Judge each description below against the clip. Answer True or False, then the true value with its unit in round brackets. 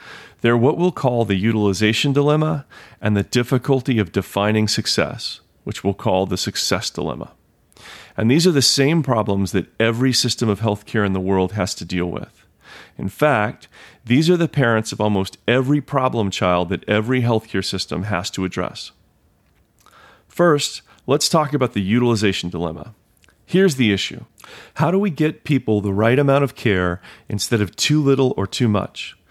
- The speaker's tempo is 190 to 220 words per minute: False (170 wpm)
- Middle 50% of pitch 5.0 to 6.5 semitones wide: True (5.5 semitones)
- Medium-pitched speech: False (110 Hz)